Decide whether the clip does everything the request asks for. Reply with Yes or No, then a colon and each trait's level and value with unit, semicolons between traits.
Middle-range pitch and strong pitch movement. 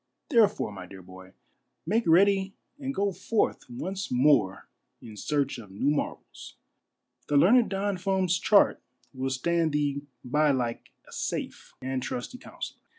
Yes: medium, 150 Hz; wide, 7.7 semitones